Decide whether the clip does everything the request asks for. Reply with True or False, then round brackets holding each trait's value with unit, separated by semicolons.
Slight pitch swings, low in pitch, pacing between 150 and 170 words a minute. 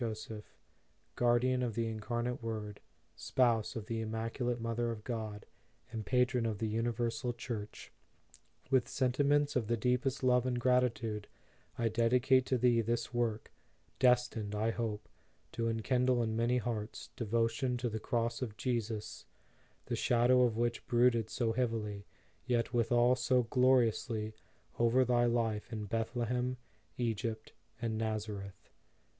False (1.9 semitones; 115 Hz; 140 wpm)